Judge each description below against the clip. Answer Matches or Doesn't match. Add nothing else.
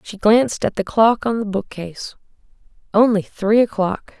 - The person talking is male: Doesn't match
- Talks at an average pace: Matches